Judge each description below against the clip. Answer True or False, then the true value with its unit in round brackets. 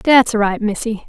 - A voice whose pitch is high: True (220 Hz)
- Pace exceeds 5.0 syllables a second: False (3.9 syllables/s)